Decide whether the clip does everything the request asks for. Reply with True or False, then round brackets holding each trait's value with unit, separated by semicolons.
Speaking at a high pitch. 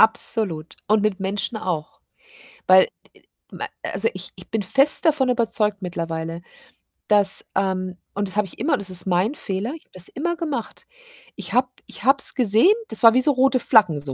True (210 Hz)